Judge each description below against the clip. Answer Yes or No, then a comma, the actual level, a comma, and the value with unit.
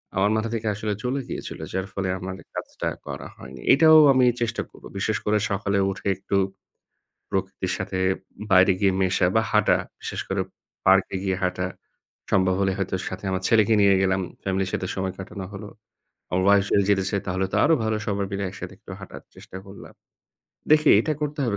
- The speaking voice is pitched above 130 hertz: No, low, 100 Hz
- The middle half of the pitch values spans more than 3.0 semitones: No, narrow, 2.4 semitones